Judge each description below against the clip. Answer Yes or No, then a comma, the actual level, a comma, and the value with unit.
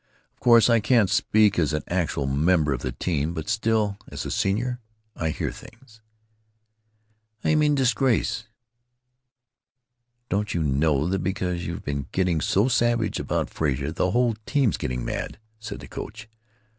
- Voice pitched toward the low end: Yes, very low, 95 Hz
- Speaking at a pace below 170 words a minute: Yes, average, 160 wpm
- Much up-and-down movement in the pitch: Yes, wide, 6.2 semitones